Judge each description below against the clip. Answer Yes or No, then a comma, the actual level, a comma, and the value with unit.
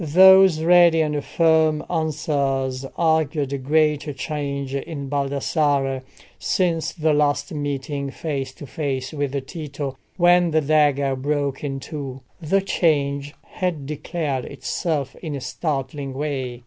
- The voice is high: No, medium, 145 Hz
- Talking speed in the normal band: No, slow, 125 wpm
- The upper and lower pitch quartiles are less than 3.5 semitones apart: Yes, narrow, 2.4 semitones